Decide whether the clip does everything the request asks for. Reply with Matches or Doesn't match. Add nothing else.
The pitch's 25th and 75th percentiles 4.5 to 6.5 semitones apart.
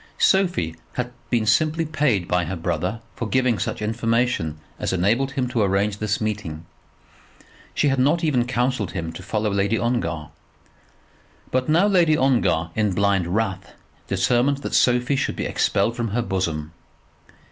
Matches